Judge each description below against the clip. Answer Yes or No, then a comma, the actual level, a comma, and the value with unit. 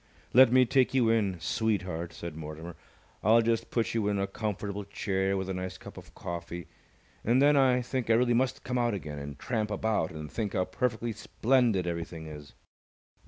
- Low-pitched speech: Yes, low, 105 Hz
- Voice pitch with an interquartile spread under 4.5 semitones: No, wide, 5.4 semitones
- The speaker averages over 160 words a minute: Yes, average, 190 wpm